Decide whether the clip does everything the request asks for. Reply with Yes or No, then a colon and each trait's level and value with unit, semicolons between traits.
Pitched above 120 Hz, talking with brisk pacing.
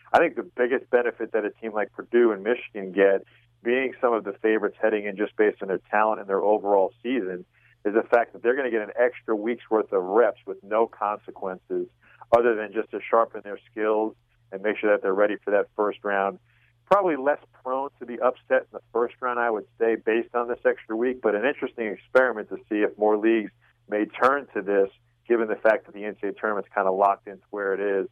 No: low, 110 Hz; fast, 230 wpm